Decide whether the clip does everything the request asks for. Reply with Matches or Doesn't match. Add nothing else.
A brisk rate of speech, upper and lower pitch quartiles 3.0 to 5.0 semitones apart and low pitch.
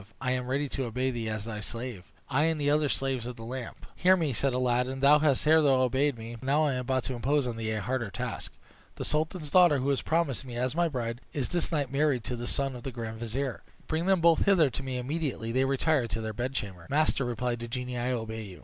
Matches